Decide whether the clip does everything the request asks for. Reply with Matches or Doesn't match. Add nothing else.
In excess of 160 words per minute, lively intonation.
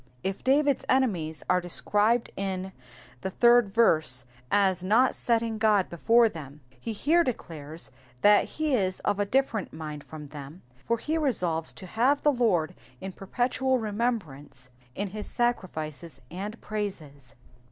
Doesn't match